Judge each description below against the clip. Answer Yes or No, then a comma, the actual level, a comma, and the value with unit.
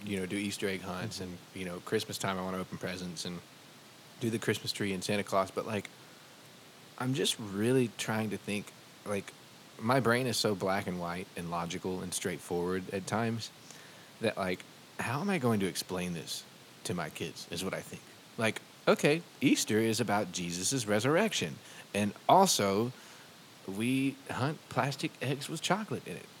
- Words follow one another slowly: No, average, 180 wpm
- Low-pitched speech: Yes, low, 105 Hz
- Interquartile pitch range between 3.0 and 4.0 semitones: No, average, 4.5 semitones